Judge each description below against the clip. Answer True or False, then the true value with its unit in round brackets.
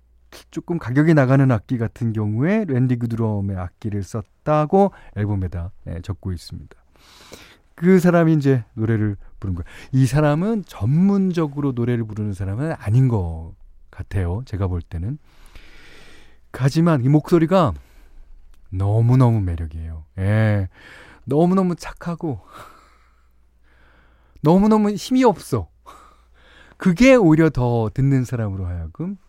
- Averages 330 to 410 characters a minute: False (260 characters per minute)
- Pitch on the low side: True (115 Hz)